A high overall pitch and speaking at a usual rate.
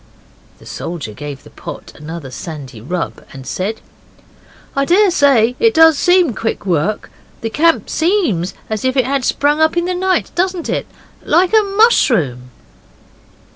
Yes: very high, 255 Hz; average, 150 wpm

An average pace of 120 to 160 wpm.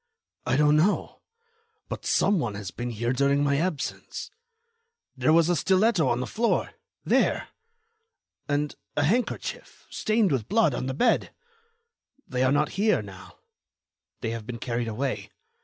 Yes: average, 145 wpm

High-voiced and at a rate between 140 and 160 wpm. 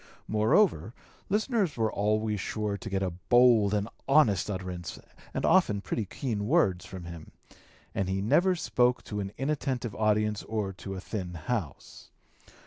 No: low, 105 Hz; average, 155 wpm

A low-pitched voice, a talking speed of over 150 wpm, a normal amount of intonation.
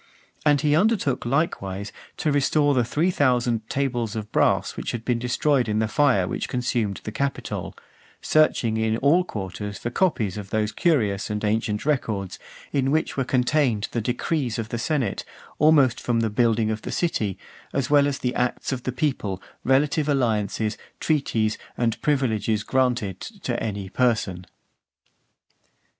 Yes: low, 120 Hz; average, 160 wpm; average, 4.7 semitones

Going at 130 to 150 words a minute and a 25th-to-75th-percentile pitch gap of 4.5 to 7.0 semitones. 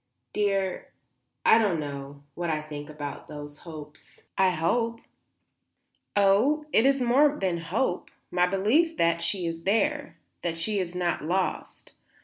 Yes: average, 140 wpm; wide, 5.4 semitones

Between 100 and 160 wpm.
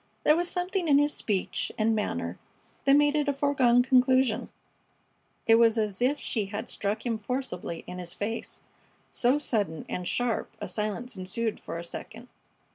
No: average, 170 wpm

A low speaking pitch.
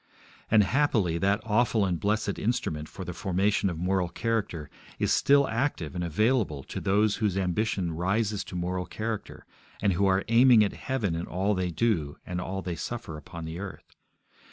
Yes: very low, 95 Hz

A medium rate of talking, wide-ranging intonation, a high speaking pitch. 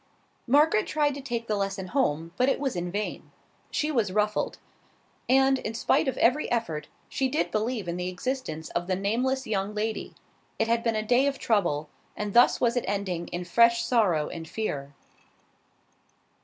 Yes: average, 180 wpm; wide, 5.8 semitones; high, 220 Hz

